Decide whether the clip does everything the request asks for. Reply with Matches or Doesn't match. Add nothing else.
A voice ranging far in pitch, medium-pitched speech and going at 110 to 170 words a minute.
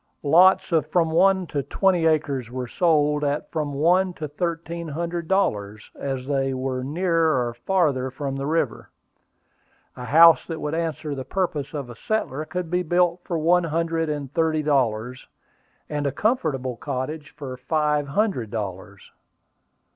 Doesn't match